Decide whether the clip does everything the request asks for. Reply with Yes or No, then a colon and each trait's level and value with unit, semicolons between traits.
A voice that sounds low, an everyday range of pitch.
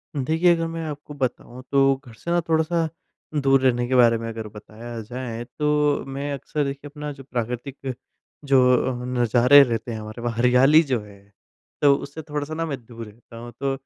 Yes: low, 130 Hz; average, 3.7 semitones